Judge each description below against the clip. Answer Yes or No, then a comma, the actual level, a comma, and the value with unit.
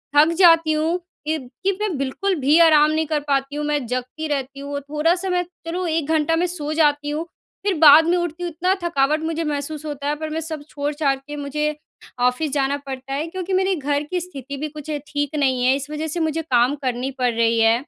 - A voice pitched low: No, very high, 300 Hz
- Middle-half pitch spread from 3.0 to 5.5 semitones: No, narrow, 2.6 semitones